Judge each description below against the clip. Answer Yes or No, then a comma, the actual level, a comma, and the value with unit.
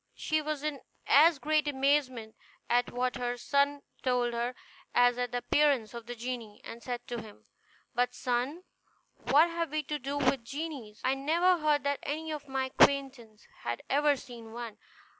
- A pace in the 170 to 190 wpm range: Yes, average, 175 wpm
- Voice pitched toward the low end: No, very high, 265 Hz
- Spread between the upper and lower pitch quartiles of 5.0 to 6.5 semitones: No, average, 3.4 semitones